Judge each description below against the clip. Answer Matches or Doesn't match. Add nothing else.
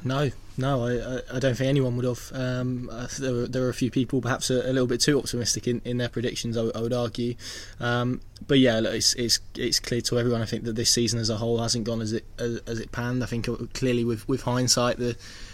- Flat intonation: Matches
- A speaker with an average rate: Doesn't match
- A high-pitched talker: Doesn't match